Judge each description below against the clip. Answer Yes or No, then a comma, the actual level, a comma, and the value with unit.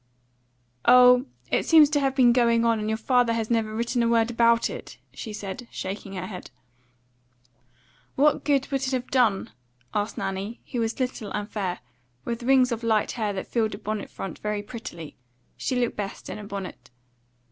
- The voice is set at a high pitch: Yes, high, 230 Hz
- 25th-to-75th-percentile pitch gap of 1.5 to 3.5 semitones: Yes, average, 3.0 semitones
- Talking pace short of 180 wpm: No, average, 185 wpm